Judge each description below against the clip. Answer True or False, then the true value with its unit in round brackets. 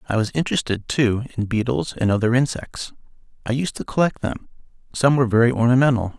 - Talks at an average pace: True (175 wpm)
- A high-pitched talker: False (120 Hz)